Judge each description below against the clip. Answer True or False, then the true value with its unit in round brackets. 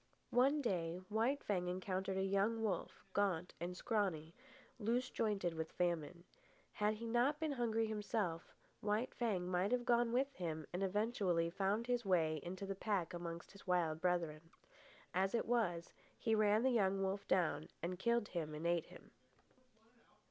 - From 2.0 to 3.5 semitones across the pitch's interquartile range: False (4.5 semitones)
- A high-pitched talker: True (195 Hz)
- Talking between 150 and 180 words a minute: True (160 wpm)